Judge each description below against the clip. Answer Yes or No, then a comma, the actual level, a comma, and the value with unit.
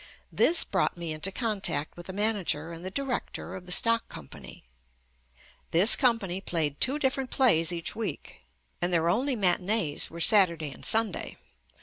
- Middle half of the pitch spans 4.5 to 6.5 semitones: Yes, average, 5.3 semitones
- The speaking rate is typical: Yes, average, 155 wpm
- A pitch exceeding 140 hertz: Yes, high, 190 Hz